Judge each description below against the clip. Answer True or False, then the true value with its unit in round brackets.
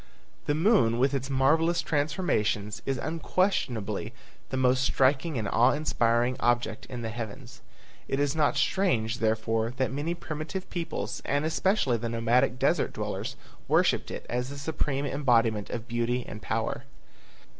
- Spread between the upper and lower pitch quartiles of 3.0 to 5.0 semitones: True (4.1 semitones)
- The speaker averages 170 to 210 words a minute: False (145 wpm)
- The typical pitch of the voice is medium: False (130 Hz)